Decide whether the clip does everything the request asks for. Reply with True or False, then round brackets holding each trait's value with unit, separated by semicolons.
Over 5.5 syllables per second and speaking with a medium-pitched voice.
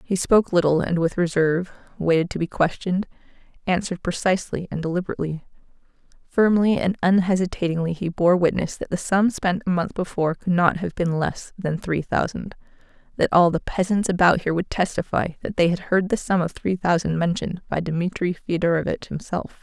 True (5.7 syllables/s; 175 Hz)